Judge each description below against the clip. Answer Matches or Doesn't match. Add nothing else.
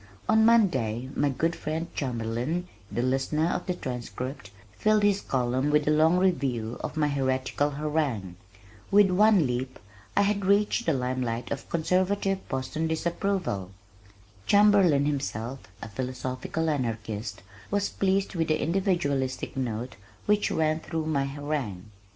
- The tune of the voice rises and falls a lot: Matches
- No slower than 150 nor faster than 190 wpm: Doesn't match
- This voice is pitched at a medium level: Matches